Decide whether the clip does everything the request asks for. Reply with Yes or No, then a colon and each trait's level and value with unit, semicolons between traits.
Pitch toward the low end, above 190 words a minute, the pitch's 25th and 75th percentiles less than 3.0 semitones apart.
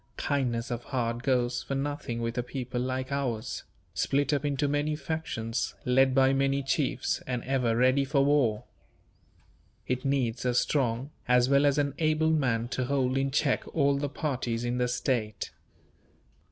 No: low, 130 Hz; average, 165 wpm; narrow, 2.5 semitones